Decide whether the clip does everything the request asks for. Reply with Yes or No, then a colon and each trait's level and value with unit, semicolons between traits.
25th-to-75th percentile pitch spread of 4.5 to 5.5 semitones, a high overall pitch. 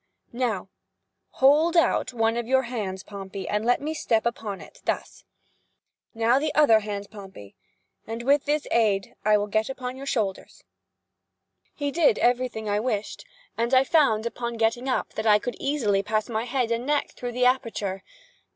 No: average, 3.5 semitones; high, 235 Hz